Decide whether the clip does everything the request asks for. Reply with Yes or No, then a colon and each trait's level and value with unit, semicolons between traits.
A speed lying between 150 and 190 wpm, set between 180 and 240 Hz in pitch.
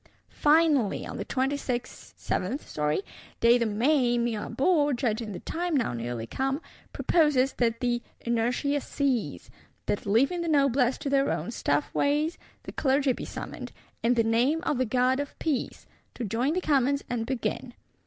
No: average, 155 wpm; very high, 255 Hz